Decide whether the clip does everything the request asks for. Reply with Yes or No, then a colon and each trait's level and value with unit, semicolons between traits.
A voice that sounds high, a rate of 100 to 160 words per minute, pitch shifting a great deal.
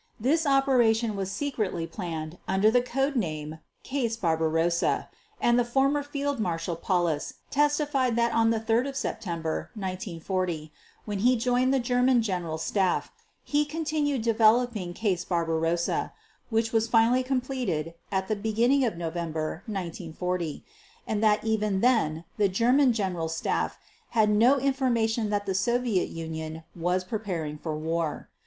Yes: high, 215 Hz; slow, 135 wpm; wide, 6.4 semitones